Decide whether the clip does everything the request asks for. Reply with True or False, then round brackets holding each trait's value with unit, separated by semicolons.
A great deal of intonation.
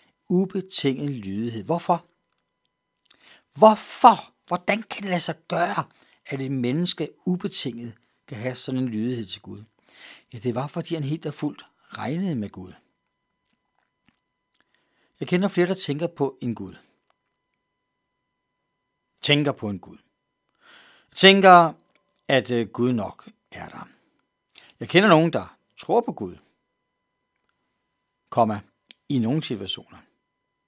True (6.9 semitones)